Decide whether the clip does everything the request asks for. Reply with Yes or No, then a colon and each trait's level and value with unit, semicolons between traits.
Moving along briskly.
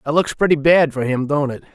Yes: fast, 275 wpm